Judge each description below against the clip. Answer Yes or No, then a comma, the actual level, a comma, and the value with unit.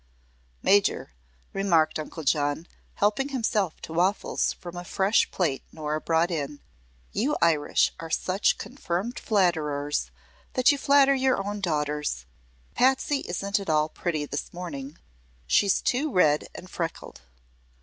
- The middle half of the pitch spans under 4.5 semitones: No, average, 5.2 semitones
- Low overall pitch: No, medium, 175 Hz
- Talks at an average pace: No, slow, 130 wpm